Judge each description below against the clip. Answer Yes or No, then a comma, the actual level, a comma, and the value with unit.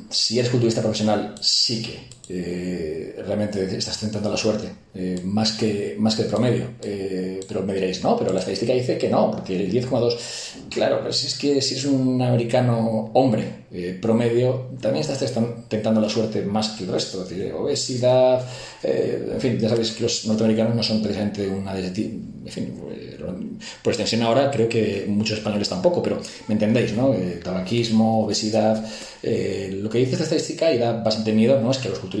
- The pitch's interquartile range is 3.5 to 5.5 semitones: No, narrow, 2.6 semitones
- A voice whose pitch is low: Yes, low, 110 Hz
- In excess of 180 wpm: Yes, fast, 190 wpm